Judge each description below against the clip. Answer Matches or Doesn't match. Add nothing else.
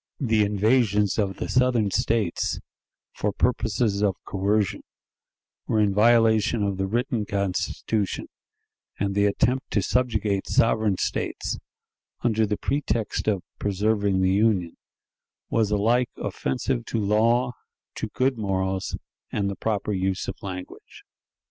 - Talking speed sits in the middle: Doesn't match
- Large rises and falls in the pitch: Doesn't match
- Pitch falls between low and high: Doesn't match